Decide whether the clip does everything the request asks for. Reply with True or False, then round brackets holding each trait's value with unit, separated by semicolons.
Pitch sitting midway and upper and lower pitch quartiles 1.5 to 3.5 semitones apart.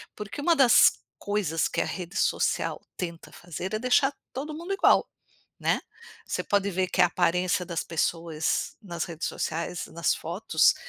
False (180 Hz; 4.2 semitones)